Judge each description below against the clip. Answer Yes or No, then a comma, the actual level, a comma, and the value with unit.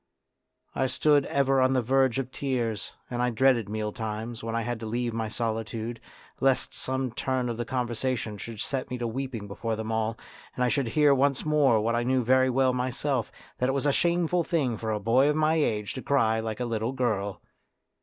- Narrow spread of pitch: No, average, 3.0 semitones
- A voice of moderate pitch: No, low, 125 Hz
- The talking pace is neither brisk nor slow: No, fast, 210 wpm